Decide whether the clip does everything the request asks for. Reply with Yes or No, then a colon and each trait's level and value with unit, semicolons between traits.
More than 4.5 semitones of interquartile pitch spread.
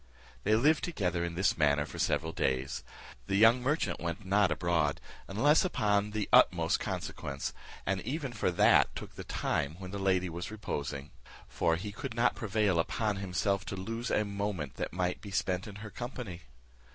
No: average, 4.0 semitones